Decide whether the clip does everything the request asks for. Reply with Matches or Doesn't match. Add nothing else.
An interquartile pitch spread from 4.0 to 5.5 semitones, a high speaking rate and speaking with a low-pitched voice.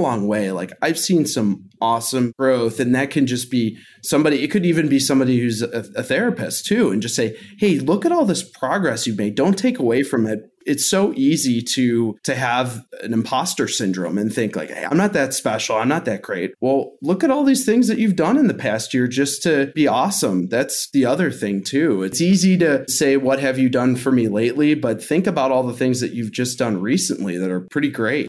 Matches